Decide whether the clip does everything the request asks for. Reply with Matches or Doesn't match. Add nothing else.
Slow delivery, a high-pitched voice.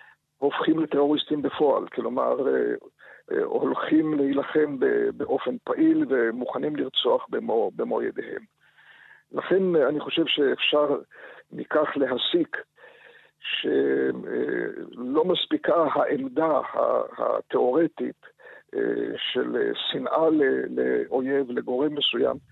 Matches